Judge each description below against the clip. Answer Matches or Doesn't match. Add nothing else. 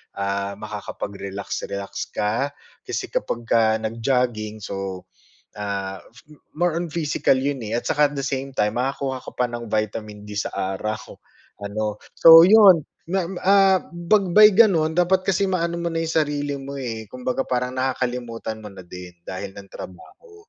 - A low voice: Matches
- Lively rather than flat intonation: Matches